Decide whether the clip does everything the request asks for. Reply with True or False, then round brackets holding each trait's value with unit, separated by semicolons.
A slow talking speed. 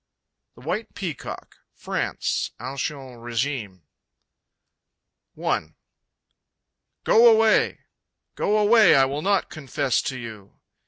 True (95 wpm)